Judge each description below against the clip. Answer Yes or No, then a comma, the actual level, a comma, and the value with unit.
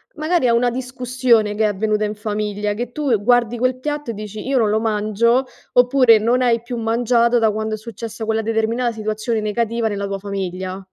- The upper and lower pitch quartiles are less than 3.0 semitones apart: Yes, narrow, 2.5 semitones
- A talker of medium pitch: No, high, 225 Hz